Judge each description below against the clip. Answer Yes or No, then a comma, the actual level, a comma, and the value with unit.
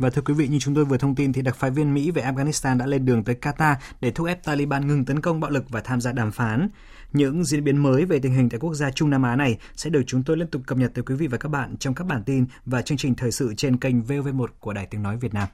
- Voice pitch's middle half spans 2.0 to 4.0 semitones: Yes, average, 2.8 semitones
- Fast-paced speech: Yes, fast, 315 wpm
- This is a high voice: No, low, 135 Hz